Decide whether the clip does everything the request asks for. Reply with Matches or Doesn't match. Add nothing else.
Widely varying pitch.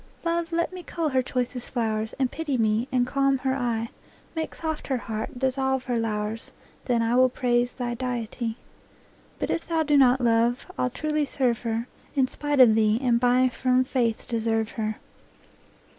Doesn't match